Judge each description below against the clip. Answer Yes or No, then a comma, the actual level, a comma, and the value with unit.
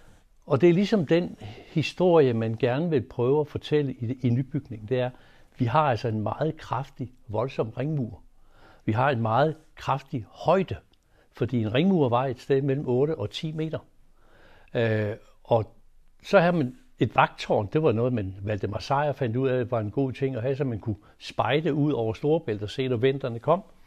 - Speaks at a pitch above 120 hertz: Yes, low, 130 Hz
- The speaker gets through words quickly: No, average, 195 wpm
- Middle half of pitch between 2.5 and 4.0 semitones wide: No, average, 4.5 semitones